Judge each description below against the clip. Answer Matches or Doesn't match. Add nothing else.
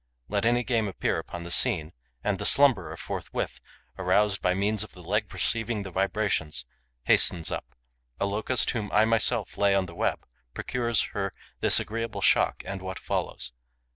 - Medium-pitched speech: Doesn't match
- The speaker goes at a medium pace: Matches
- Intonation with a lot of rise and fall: Doesn't match